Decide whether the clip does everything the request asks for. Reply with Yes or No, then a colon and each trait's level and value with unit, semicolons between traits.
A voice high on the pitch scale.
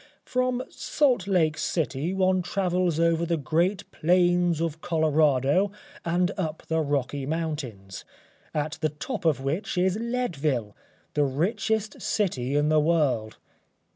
No: medium, 165 Hz